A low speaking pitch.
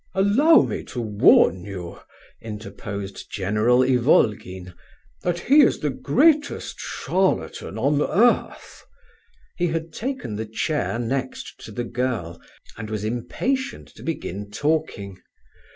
Yes: low, 125 Hz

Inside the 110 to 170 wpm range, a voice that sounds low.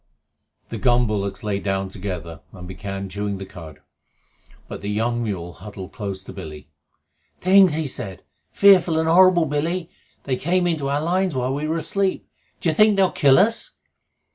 Yes: average, 165 wpm; low, 125 Hz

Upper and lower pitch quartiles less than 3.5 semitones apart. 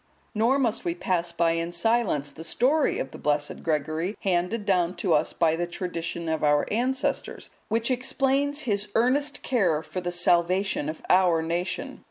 No: wide, 5.6 semitones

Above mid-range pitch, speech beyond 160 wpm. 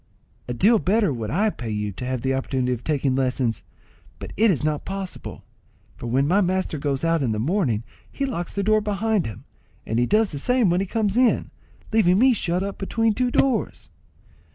No: medium, 175 Hz; fast, 205 wpm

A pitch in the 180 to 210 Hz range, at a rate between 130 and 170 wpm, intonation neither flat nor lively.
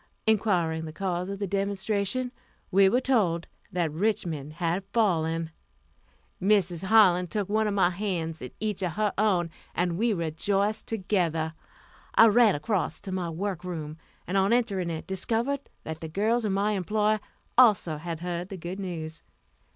Yes: high, 190 Hz; average, 160 wpm; average, 3.9 semitones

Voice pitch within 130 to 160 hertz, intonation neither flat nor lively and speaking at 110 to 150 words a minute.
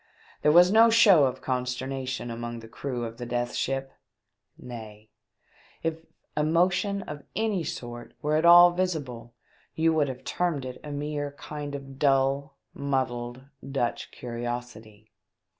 Yes: low, 135 Hz; average, 4.5 semitones; average, 140 wpm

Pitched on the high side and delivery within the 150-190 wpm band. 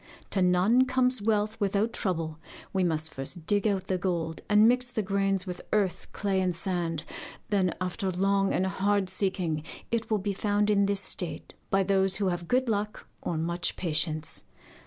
Yes: high, 195 Hz; average, 180 wpm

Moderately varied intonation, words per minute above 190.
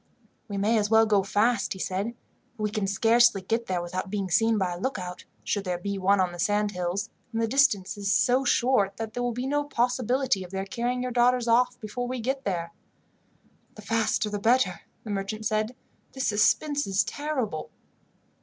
Yes: average, 3.9 semitones; average, 200 wpm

